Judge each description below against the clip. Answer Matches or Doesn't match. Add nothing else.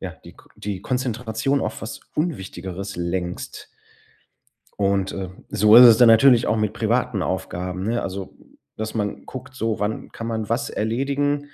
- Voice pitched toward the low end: Matches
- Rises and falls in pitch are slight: Doesn't match